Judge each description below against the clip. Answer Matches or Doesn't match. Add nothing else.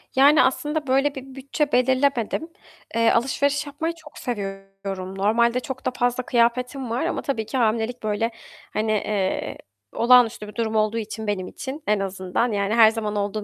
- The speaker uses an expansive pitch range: Doesn't match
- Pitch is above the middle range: Matches